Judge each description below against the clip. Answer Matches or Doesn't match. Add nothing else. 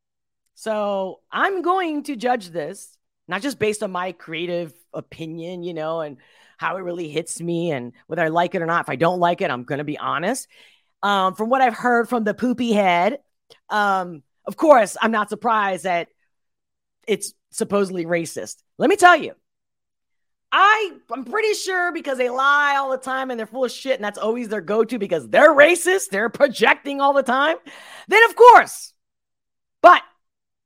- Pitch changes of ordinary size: Doesn't match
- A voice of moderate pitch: Doesn't match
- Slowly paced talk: Doesn't match